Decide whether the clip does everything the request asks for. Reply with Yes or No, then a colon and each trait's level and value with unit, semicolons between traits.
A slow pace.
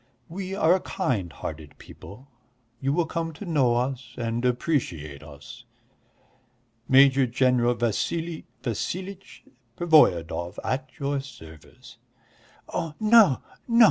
Yes: slow, 110 wpm